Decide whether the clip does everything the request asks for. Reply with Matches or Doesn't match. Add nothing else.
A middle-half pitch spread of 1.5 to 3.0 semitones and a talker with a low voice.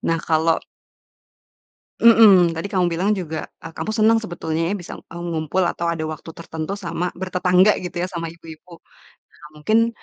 Doesn't match